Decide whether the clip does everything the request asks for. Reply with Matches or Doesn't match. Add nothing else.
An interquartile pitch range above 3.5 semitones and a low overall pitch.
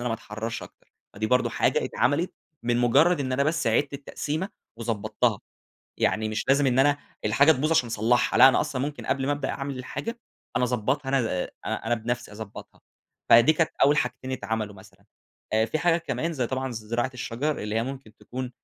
Matches